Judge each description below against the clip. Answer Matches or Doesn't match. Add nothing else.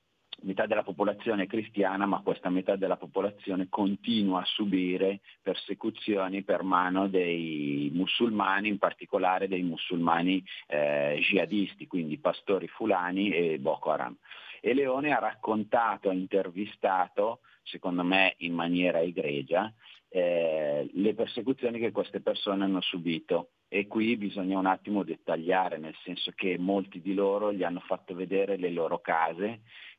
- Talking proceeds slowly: Doesn't match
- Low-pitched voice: Matches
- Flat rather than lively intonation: Matches